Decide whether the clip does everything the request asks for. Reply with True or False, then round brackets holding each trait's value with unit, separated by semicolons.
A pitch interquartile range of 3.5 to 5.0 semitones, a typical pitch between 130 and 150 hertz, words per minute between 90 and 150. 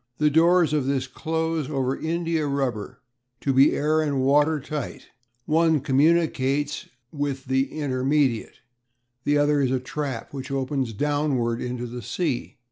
False (2.7 semitones; 140 Hz; 140 wpm)